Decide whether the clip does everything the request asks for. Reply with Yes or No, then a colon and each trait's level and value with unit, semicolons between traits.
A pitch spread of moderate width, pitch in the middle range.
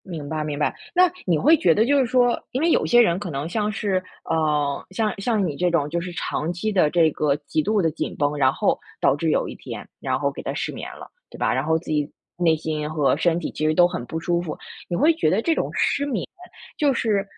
No: wide, 5.7 semitones; medium, 170 Hz